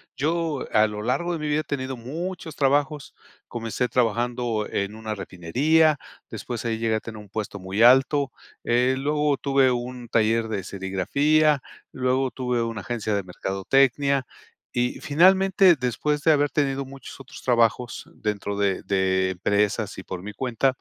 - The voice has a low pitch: Yes, low, 125 Hz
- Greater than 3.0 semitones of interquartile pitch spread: Yes, average, 4.9 semitones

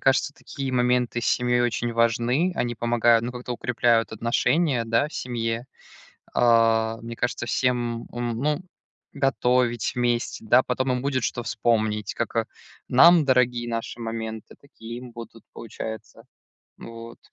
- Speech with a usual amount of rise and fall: No, narrow, 1.5 semitones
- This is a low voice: Yes, low, 120 Hz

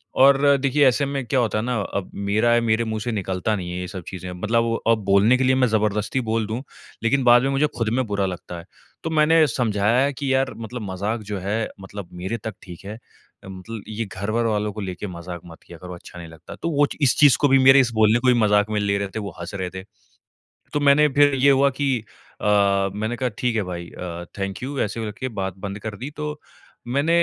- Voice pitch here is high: No, low, 110 Hz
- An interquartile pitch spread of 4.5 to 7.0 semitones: Yes, average, 4.8 semitones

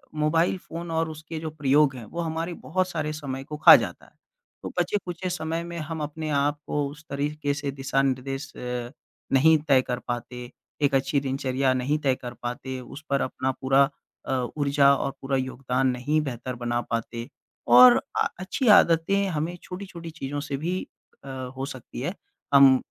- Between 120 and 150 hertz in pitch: Yes, medium, 140 Hz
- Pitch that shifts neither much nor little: Yes, average, 3.3 semitones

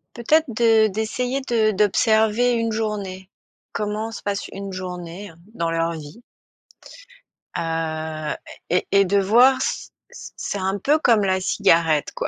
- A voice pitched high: Yes, high, 200 Hz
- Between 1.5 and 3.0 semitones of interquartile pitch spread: No, average, 4.1 semitones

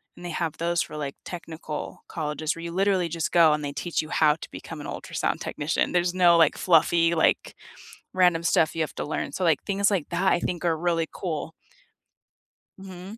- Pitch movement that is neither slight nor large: No, narrow, 2.0 semitones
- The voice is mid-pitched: Yes, medium, 170 Hz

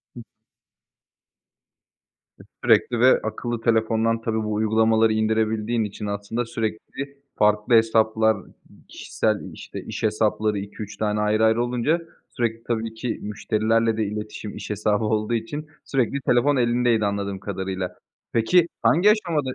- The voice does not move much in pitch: Yes, narrow, 1.9 semitones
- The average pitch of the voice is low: Yes, low, 110 Hz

